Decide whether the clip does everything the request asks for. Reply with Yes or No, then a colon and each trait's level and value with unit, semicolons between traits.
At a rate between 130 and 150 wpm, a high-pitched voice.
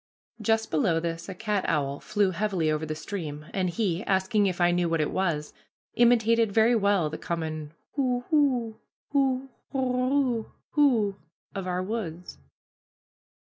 Yes: average, 145 wpm; high, 195 Hz